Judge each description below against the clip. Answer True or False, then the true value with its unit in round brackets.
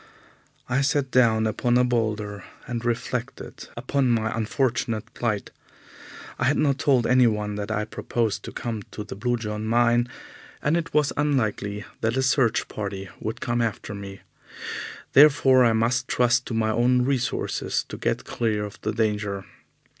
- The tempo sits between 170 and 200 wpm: False (160 wpm)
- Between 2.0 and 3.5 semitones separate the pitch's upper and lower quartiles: True (2.8 semitones)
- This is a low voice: True (115 Hz)